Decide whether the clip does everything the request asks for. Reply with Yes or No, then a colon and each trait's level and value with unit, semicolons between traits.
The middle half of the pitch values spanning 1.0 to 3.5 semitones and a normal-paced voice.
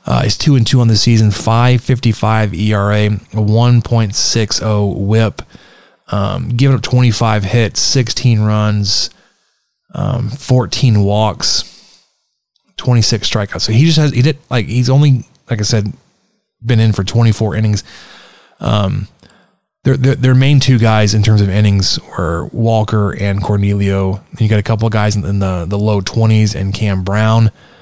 Yes: average, 2.8 semitones; average, 160 wpm